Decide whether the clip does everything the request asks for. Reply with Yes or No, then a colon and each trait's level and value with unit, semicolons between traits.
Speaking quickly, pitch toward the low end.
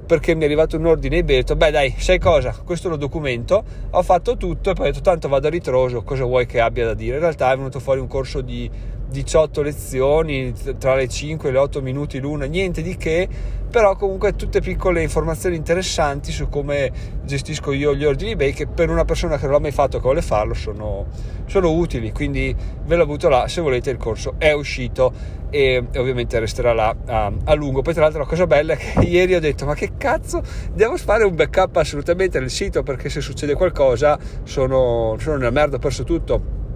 No: fast, 215 wpm; medium, 145 Hz